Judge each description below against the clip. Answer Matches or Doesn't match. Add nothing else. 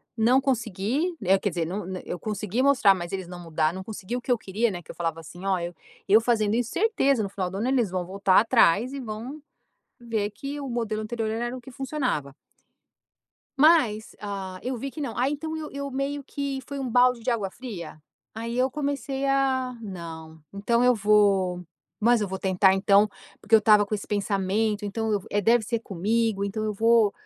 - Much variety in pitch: Doesn't match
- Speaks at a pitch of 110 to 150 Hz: Doesn't match